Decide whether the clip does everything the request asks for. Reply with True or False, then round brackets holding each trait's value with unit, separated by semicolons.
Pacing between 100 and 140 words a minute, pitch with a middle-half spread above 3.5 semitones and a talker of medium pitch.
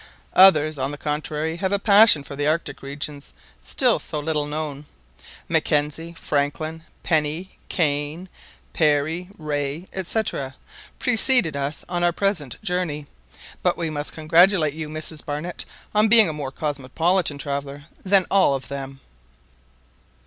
False (135 wpm; 3.2 semitones; 155 Hz)